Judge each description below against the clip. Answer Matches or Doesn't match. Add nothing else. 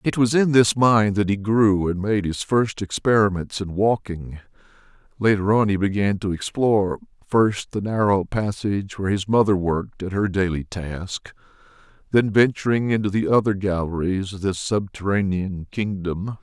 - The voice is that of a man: Matches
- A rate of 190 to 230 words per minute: Doesn't match